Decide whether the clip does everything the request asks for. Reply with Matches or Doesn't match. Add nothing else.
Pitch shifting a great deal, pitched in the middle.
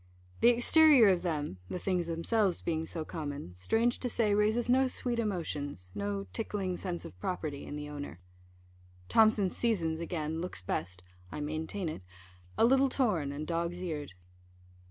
Matches